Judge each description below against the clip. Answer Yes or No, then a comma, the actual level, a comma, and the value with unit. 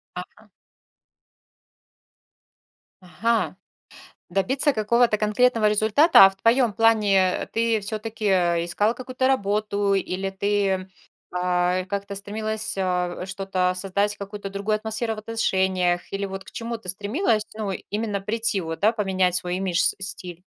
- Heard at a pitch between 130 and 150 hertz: No, high, 200 Hz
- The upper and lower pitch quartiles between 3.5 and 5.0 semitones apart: No, average, 2.7 semitones